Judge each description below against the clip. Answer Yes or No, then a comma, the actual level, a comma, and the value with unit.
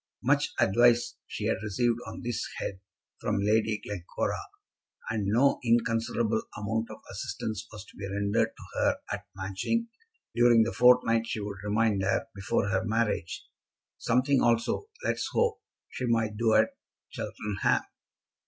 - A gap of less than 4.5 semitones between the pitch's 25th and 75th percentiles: Yes, narrow, 2.4 semitones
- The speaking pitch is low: Yes, low, 110 Hz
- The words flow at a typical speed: Yes, average, 145 wpm